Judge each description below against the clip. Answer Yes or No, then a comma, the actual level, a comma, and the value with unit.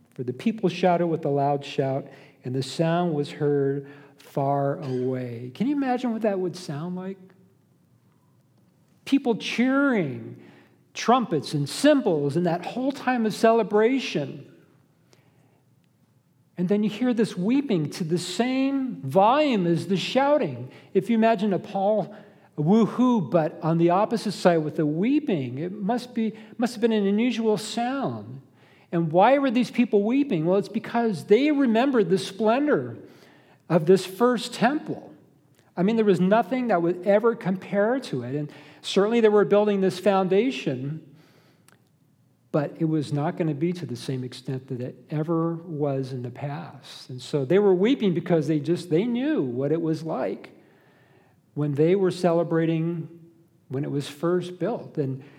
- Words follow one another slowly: No, average, 160 wpm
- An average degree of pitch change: No, wide, 6.9 semitones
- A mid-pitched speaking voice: Yes, medium, 175 Hz